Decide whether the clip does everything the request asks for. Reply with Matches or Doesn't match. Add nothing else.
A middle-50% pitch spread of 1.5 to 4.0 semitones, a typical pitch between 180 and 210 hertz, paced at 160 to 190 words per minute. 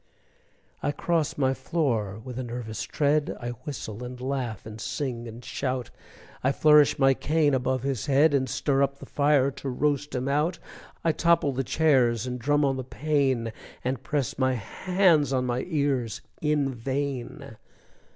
Doesn't match